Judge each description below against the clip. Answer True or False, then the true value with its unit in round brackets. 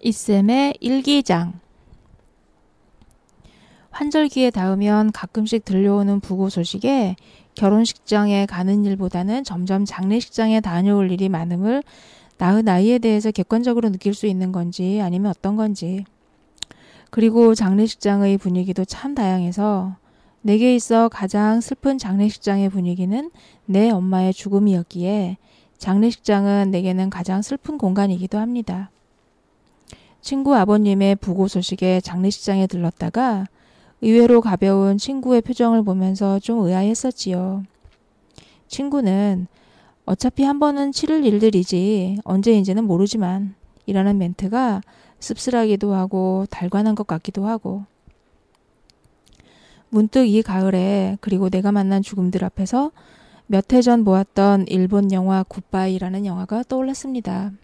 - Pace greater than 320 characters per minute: False (285 characters per minute)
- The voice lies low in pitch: False (200 Hz)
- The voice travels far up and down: False (3.1 semitones)